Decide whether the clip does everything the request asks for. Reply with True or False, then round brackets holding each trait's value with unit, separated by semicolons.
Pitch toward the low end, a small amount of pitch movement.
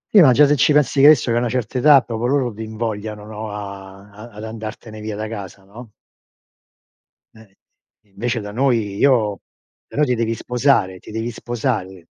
False (110 Hz; 3.1 semitones)